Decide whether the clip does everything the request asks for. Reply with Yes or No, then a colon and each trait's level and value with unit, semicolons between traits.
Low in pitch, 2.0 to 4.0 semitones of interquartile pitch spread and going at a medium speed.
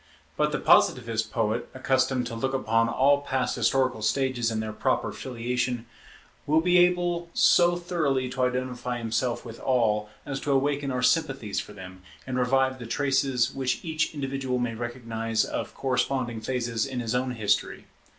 Yes: low, 125 Hz; average, 2.7 semitones; average, 160 wpm